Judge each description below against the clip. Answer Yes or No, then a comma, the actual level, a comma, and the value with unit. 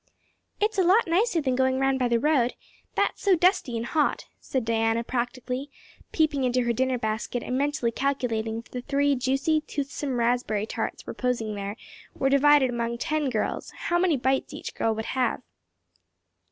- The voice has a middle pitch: No, very high, 260 Hz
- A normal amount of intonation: Yes, average, 3.6 semitones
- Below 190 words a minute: Yes, average, 175 wpm